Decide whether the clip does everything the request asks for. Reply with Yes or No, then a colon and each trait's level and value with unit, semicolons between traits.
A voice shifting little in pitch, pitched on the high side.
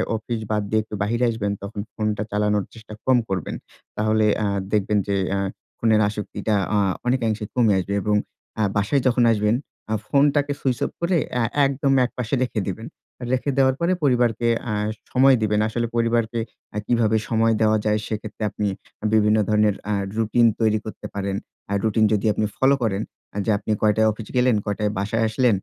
No: narrow, 2.3 semitones; low, 110 Hz